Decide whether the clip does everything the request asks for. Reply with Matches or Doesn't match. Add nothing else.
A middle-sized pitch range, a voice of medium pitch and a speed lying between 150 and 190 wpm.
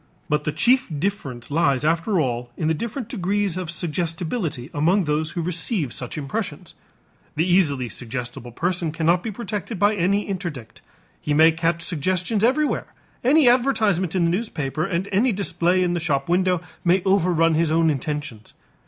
Matches